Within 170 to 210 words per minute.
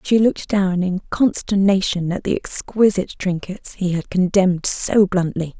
No: average, 150 wpm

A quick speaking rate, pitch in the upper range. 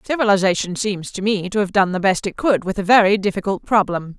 Yes: fast, 230 wpm; high, 195 Hz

